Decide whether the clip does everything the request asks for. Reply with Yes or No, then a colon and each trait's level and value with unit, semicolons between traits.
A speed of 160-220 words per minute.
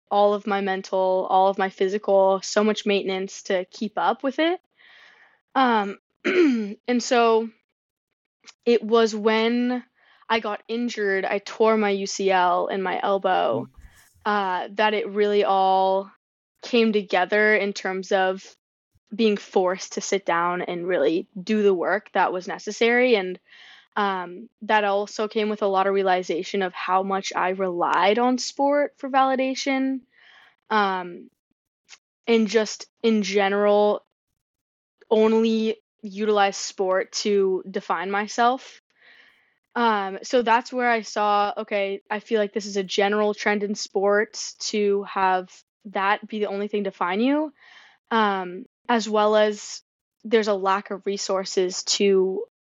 No: average, 140 wpm